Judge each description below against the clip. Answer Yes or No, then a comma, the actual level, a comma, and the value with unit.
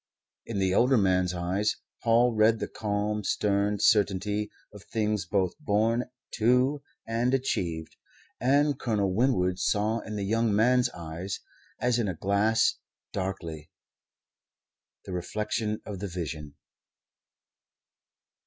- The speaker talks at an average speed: No, slow, 120 wpm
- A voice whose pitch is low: Yes, low, 105 Hz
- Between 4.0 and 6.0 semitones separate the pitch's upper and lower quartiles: No, average, 3.4 semitones